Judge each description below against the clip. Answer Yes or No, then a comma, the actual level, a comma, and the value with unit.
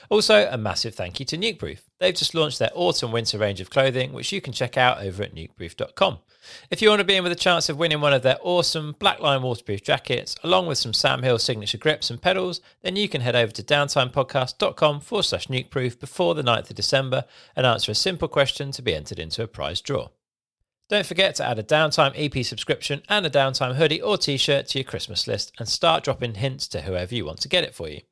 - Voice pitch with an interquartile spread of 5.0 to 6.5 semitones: Yes, wide, 5.5 semitones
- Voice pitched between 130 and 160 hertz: Yes, low, 135 Hz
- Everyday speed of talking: No, fast, 235 wpm